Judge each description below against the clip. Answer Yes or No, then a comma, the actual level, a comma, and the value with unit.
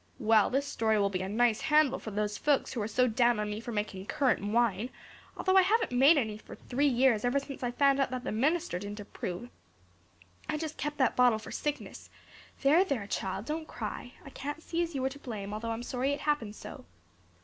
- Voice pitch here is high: Yes, high, 245 Hz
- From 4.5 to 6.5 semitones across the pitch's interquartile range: Yes, average, 4.8 semitones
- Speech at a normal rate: No, fast, 225 wpm